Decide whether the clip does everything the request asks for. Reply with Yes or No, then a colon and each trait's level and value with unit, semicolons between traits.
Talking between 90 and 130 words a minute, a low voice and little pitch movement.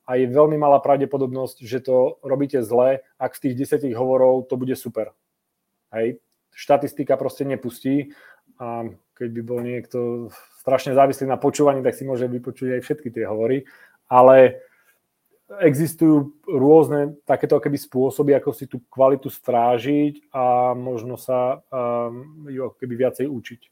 No: average, 140 wpm; low, 130 Hz; narrow, 2.2 semitones